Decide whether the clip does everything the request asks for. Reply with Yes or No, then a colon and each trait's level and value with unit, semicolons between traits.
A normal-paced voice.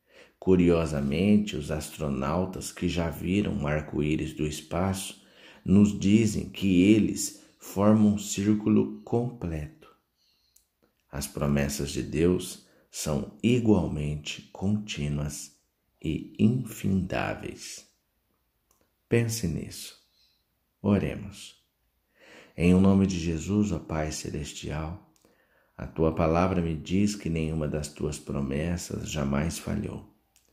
No: slow, 100 wpm